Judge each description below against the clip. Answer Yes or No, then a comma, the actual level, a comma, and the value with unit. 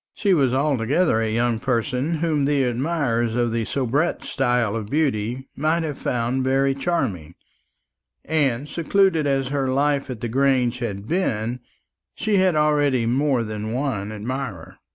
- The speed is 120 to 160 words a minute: Yes, average, 150 wpm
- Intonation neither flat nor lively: Yes, average, 4.1 semitones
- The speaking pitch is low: Yes, low, 130 Hz